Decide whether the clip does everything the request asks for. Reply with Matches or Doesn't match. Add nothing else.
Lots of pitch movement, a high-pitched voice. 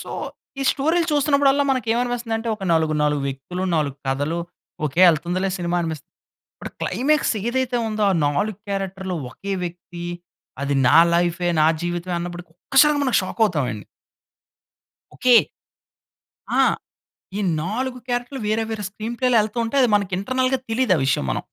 Matches